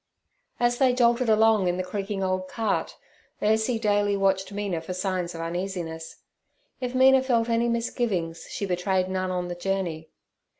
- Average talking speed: Yes, average, 160 wpm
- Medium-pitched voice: No, high, 195 Hz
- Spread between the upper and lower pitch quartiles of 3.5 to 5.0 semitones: Yes, average, 4.0 semitones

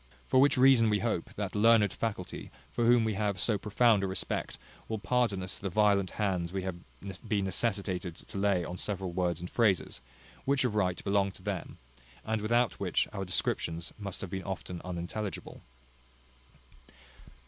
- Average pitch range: Yes, average, 3.2 semitones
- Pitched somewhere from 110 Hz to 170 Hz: No, low, 100 Hz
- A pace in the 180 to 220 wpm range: No, average, 170 wpm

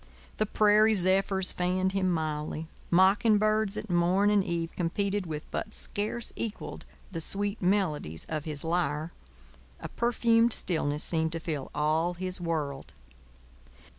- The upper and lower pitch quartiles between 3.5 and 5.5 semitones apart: Yes, average, 4.1 semitones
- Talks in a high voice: No, medium, 180 Hz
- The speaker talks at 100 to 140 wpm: Yes, slow, 135 wpm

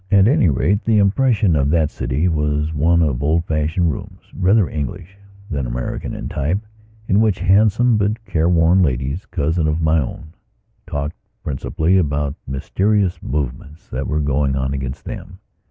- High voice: No, very low, 80 Hz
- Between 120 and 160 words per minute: Yes, average, 155 wpm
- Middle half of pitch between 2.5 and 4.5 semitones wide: No, average, 5.0 semitones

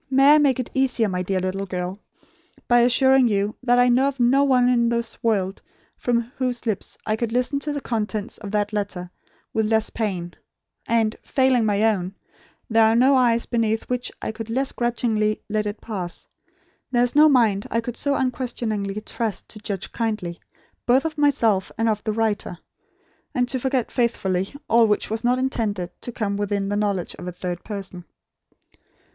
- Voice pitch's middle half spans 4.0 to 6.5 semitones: No, average, 3.3 semitones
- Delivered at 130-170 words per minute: No, average, 185 wpm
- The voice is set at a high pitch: Yes, high, 225 Hz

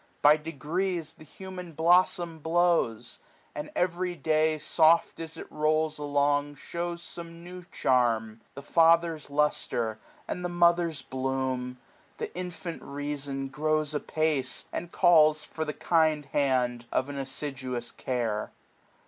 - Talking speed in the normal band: No, slow, 130 wpm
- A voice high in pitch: No, medium, 155 Hz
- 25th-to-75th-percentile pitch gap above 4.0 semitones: No, average, 3.7 semitones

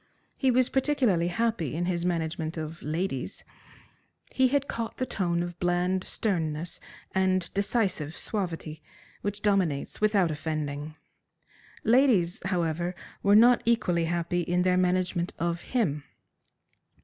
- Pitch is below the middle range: No, medium, 180 Hz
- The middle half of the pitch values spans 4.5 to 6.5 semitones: No, average, 3.8 semitones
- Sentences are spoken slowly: Yes, slow, 125 wpm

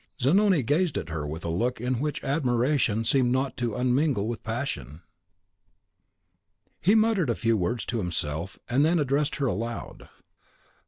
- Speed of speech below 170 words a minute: Yes, average, 150 wpm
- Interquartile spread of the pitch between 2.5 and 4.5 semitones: No, average, 4.9 semitones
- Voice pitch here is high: No, low, 125 Hz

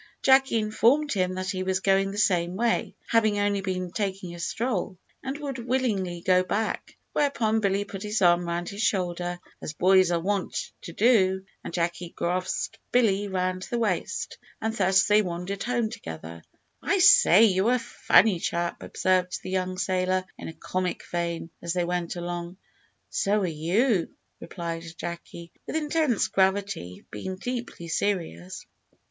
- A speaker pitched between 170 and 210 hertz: Yes, high, 190 Hz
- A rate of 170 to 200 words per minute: No, average, 160 wpm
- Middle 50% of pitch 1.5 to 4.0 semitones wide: Yes, average, 3.6 semitones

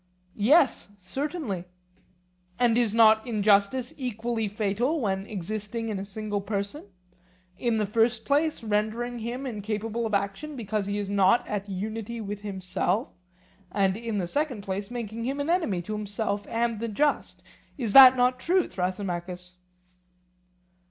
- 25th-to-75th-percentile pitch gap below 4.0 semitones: Yes, average, 3.2 semitones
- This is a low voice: No, high, 215 Hz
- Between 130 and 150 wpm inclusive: Yes, average, 145 wpm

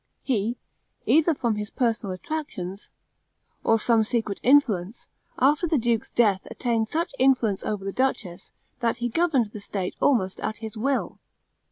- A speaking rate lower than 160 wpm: Yes, average, 150 wpm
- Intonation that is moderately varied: Yes, average, 4.2 semitones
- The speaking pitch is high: Yes, high, 230 Hz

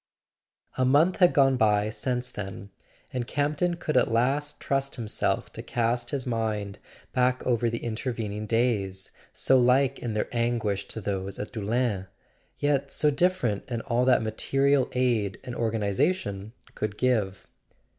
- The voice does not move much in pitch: No, average, 3.8 semitones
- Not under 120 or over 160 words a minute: Yes, average, 145 wpm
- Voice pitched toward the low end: Yes, low, 120 Hz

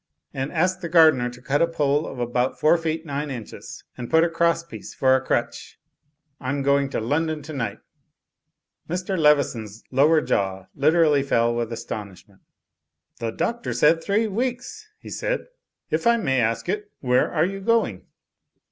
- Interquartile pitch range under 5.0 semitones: No, average, 5.3 semitones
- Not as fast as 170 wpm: No, average, 175 wpm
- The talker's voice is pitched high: No, medium, 150 Hz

